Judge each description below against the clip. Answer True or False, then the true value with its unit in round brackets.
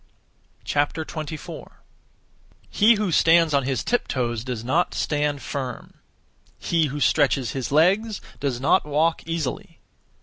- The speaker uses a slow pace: True (115 wpm)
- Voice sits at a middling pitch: True (150 Hz)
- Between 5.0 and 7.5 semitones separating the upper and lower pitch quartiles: False (3.9 semitones)